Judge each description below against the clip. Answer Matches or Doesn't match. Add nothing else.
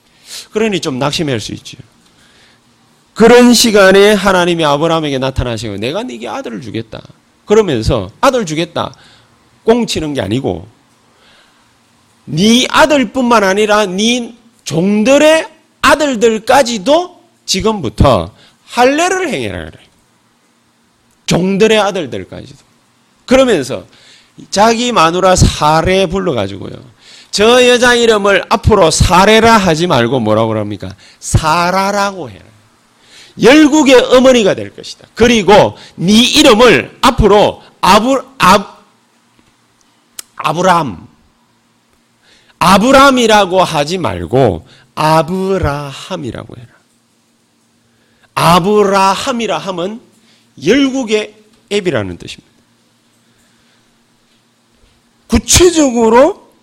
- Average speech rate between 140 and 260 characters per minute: Matches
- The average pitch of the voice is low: Doesn't match